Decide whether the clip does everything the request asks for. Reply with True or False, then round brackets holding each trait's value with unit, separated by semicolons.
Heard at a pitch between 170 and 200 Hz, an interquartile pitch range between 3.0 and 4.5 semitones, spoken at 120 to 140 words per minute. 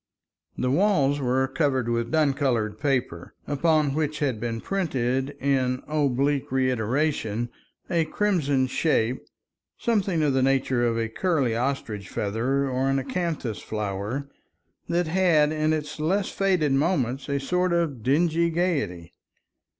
False (140 Hz; 4.1 semitones; 135 wpm)